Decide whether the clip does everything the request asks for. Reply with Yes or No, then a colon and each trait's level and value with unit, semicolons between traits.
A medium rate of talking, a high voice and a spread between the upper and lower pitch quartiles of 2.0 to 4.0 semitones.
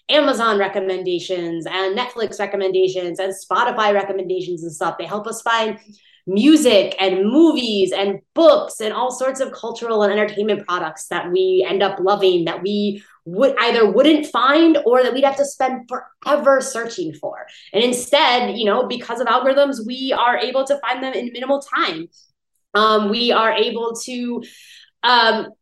No: average, 160 wpm; high, 225 Hz; average, 5.1 semitones